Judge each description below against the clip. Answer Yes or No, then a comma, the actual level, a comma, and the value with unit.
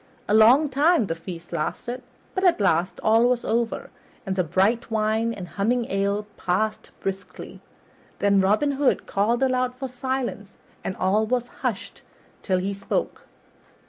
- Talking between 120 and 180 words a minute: Yes, average, 150 wpm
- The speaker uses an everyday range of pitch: Yes, average, 4.3 semitones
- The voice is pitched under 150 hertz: No, high, 220 Hz